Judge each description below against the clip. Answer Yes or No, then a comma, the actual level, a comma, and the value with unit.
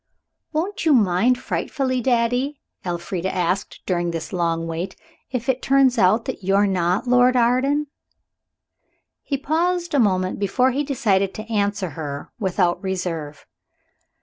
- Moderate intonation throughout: No, wide, 6.2 semitones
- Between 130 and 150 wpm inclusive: Yes, slow, 135 wpm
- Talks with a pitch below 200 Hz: No, high, 205 Hz